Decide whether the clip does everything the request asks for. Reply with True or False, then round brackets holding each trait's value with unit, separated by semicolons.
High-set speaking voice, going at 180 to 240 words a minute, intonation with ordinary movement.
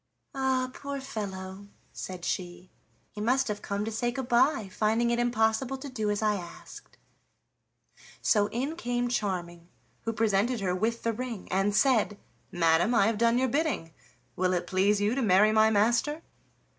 False (220 Hz; 170 wpm; 3.8 semitones)